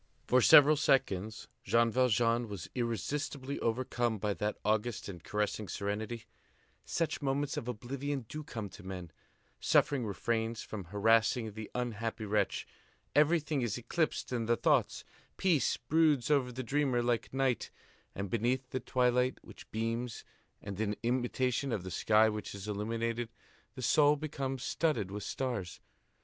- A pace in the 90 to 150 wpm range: Yes, average, 145 wpm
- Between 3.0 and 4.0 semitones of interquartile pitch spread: Yes, average, 3.6 semitones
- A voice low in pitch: Yes, low, 120 Hz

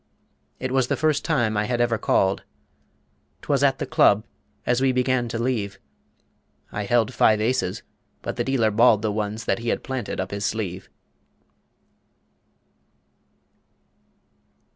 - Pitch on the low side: Yes, low, 115 Hz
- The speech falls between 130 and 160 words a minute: Yes, average, 140 wpm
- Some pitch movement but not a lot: Yes, average, 3.4 semitones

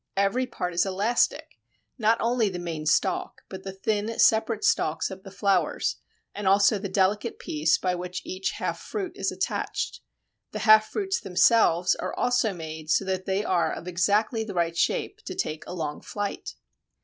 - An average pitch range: Yes, average, 3.4 semitones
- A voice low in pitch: No, high, 195 Hz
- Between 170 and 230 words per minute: Yes, average, 175 wpm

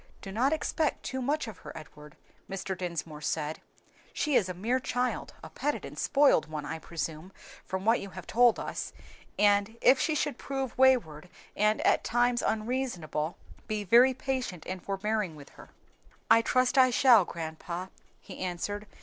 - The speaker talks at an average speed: Yes, average, 165 wpm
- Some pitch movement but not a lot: No, wide, 6.5 semitones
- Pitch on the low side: No, high, 210 Hz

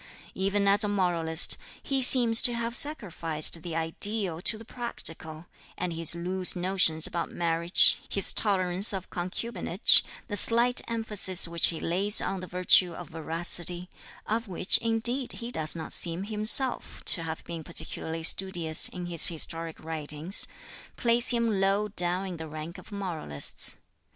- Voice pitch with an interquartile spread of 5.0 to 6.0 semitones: No, average, 4.1 semitones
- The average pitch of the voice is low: No, medium, 180 Hz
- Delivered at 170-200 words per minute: No, average, 150 wpm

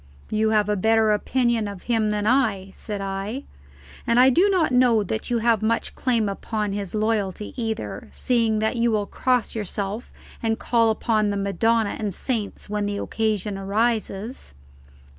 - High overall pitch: Yes, high, 220 Hz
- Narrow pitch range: Yes, narrow, 2.2 semitones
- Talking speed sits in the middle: Yes, average, 165 wpm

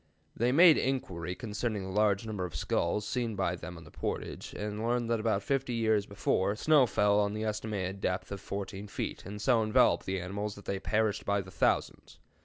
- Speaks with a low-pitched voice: Yes, low, 105 Hz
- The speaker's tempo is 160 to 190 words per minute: No, average, 200 wpm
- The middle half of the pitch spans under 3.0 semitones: Yes, narrow, 2.6 semitones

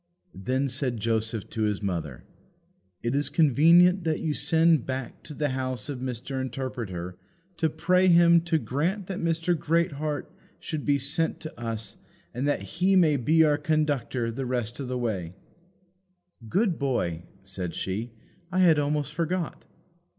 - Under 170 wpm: Yes, average, 150 wpm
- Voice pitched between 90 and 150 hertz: Yes, medium, 140 Hz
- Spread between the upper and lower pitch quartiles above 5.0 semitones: Yes, wide, 5.5 semitones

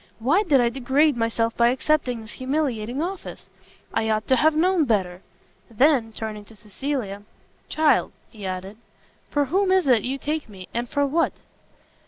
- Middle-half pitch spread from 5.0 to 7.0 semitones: Yes, wide, 5.4 semitones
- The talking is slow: No, average, 165 wpm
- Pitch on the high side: Yes, very high, 250 Hz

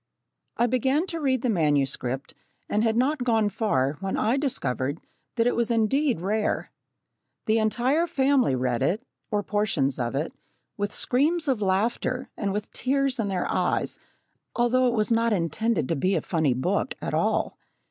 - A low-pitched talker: No, high, 220 Hz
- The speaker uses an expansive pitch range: Yes, wide, 6.7 semitones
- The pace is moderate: Yes, average, 170 wpm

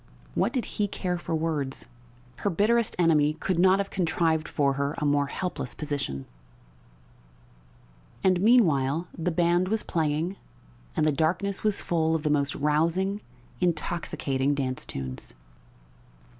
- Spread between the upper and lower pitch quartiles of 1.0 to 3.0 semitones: No, average, 4.1 semitones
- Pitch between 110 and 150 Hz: No, medium, 160 Hz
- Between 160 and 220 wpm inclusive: No, slow, 135 wpm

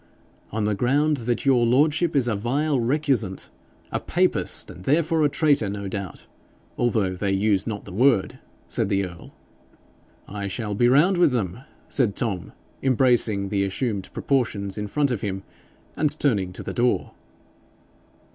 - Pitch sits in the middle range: No, low, 115 Hz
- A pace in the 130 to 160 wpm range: Yes, average, 155 wpm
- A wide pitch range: Yes, wide, 5.7 semitones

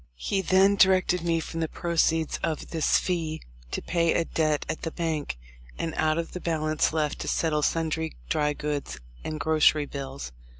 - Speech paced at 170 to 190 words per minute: Yes, average, 175 wpm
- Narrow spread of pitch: Yes, narrow, 1.7 semitones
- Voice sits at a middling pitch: Yes, medium, 160 Hz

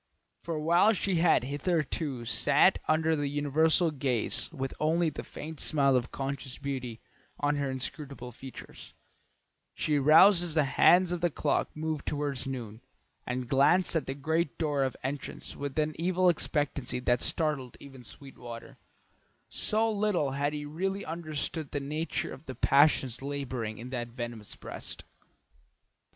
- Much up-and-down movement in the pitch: No, average, 3.4 semitones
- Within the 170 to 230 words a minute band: No, average, 150 wpm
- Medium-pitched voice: Yes, medium, 145 Hz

